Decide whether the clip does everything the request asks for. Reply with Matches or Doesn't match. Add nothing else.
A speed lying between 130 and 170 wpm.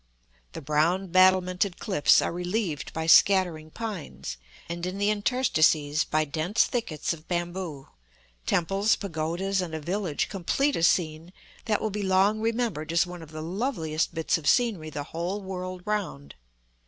Matches